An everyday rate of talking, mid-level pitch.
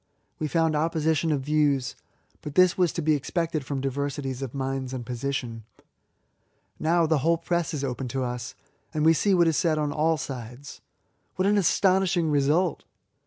Yes: average, 170 wpm; medium, 150 Hz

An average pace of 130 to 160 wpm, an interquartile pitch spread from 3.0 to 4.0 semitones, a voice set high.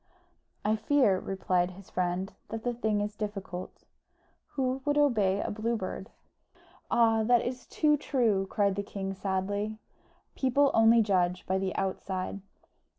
Yes: average, 145 wpm; average, 3.7 semitones; high, 210 Hz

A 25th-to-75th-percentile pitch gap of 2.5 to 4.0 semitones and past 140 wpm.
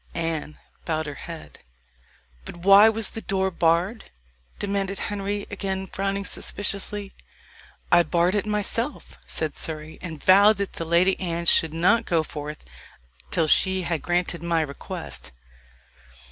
No: average, 3.4 semitones; slow, 135 wpm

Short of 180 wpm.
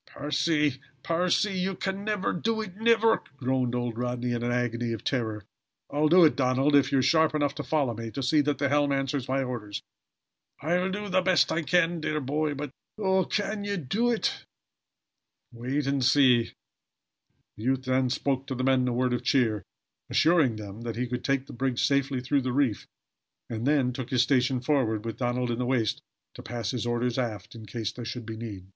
No: fast, 205 wpm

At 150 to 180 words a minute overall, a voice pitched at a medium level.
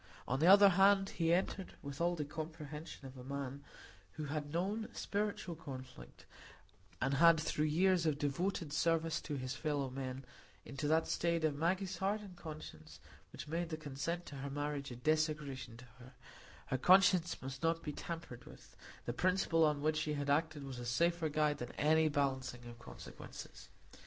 Yes: average, 175 wpm; medium, 155 Hz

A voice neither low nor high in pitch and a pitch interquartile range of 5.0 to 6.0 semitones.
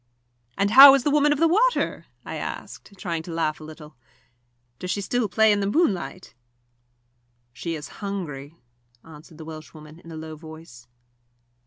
Yes: medium, 170 Hz; wide, 5.5 semitones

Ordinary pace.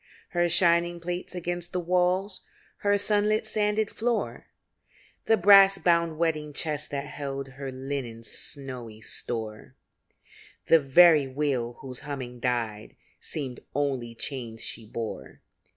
No: slow, 120 wpm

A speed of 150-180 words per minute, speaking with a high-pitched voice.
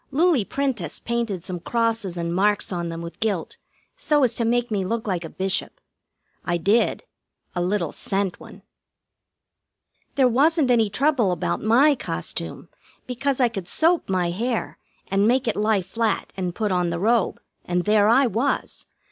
Yes: average, 165 wpm; high, 215 Hz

